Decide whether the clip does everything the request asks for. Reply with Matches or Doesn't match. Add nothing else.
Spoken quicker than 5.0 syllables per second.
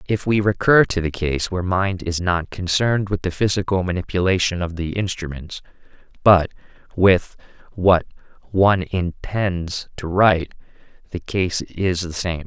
Doesn't match